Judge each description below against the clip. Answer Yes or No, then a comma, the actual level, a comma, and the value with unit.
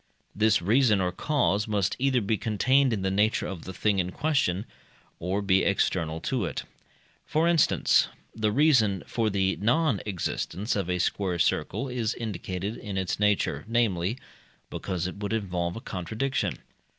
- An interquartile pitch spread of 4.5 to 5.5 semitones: No, average, 3.8 semitones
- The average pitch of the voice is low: Yes, low, 105 Hz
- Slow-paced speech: No, average, 160 wpm